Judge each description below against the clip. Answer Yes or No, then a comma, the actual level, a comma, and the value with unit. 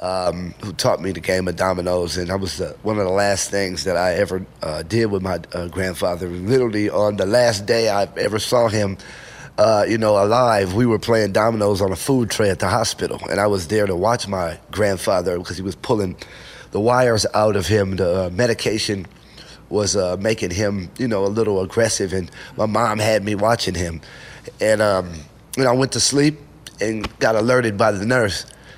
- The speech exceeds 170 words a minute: Yes, fast, 205 wpm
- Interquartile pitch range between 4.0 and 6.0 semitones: No, average, 3.1 semitones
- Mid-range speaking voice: No, low, 100 Hz